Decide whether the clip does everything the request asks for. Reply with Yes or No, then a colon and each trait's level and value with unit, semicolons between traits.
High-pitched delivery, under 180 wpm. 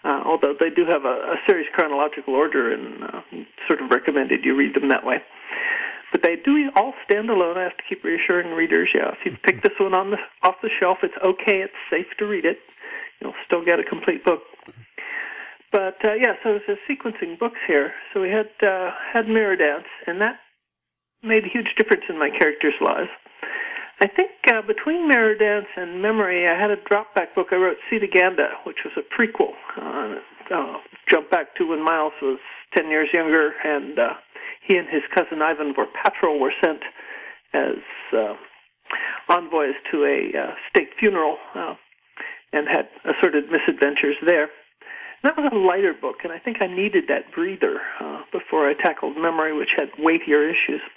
No: high, 210 Hz; average, 185 wpm